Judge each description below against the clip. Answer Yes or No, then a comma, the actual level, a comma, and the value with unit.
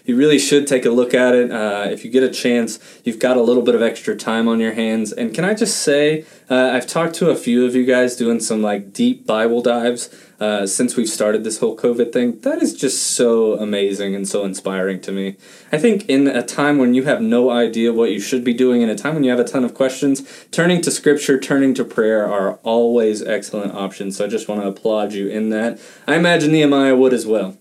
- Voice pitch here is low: Yes, low, 120 Hz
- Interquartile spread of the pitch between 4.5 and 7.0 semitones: No, average, 4.1 semitones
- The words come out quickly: Yes, fast, 245 wpm